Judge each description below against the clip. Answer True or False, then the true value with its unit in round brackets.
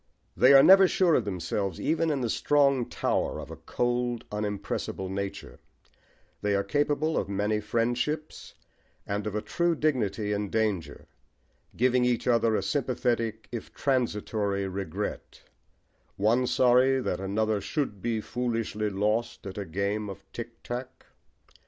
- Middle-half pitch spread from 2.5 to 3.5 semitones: False (3.9 semitones)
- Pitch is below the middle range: True (115 Hz)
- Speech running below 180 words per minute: True (140 wpm)